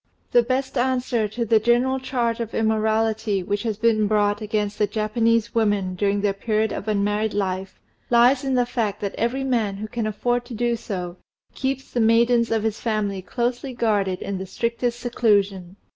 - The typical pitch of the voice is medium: No, high, 220 Hz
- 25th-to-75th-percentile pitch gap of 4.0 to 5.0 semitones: No, average, 2.7 semitones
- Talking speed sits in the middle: Yes, average, 180 wpm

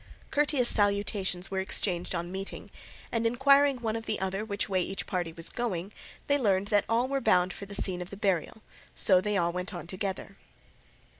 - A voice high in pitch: Yes, high, 200 Hz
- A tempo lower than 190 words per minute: No, average, 195 wpm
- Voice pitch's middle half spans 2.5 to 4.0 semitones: Yes, average, 3.6 semitones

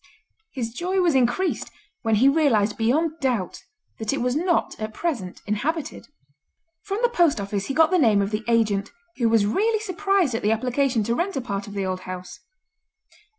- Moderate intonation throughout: No, wide, 7.5 semitones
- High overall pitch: Yes, high, 245 Hz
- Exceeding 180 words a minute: Yes, average, 190 wpm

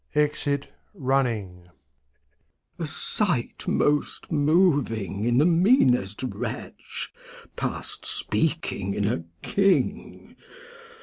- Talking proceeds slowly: Yes, slow, 85 wpm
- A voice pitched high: No, medium, 140 Hz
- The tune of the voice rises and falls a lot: Yes, wide, 7.0 semitones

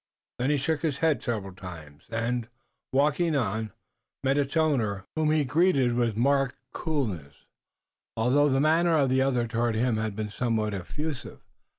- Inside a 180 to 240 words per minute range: No, average, 160 wpm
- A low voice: Yes, low, 125 Hz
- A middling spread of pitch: Yes, average, 5.0 semitones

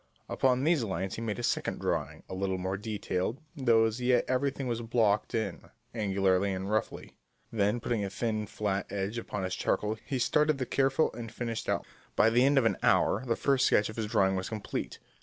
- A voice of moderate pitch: No, low, 110 Hz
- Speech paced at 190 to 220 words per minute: Yes, fast, 205 wpm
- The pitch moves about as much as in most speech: Yes, average, 3.7 semitones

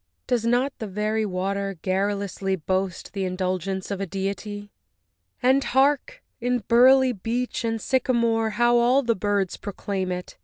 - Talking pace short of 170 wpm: Yes, average, 145 wpm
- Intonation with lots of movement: No, average, 3.8 semitones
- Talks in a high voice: Yes, high, 205 Hz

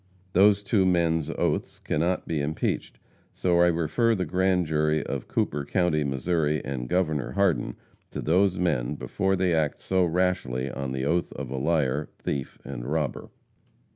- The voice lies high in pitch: No, very low, 80 Hz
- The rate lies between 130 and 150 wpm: No, average, 160 wpm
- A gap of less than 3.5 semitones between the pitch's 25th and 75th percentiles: No, average, 4.4 semitones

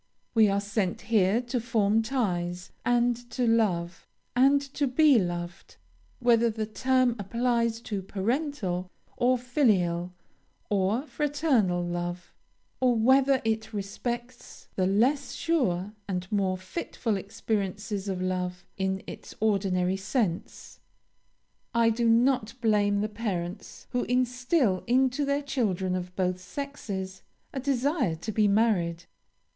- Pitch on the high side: Yes, high, 215 Hz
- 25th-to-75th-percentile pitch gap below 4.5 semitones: No, average, 4.8 semitones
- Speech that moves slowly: Yes, slow, 125 wpm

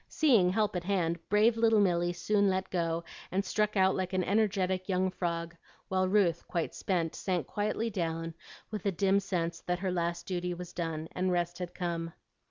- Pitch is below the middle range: No, medium, 185 Hz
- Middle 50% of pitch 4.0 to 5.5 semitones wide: No, narrow, 2.5 semitones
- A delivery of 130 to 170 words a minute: No, average, 185 wpm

